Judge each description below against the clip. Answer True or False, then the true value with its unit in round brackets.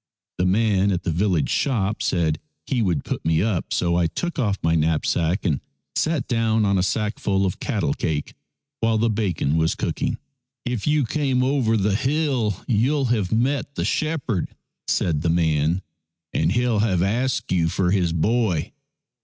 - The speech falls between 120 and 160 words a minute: False (170 wpm)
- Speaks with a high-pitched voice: False (100 Hz)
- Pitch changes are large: True (5.9 semitones)